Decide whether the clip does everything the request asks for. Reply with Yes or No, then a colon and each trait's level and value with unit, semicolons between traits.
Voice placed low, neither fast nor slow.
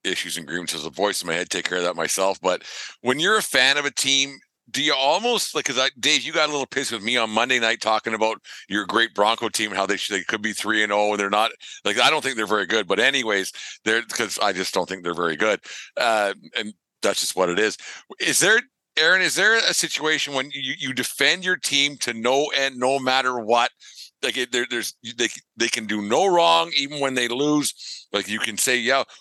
No: low, 120 Hz; fast, 250 wpm